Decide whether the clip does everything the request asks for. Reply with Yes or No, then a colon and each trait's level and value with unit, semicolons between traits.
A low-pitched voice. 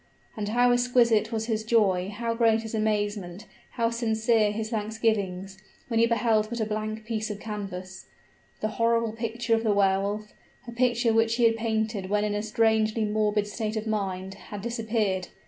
No: high, 220 Hz